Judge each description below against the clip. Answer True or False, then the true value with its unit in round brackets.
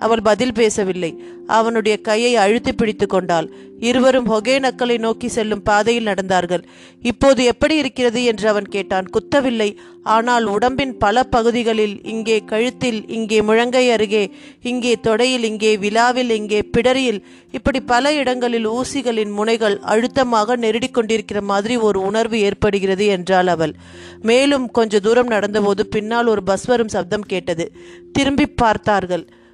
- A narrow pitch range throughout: False (3.0 semitones)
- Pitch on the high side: True (225 Hz)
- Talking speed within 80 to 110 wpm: False (125 wpm)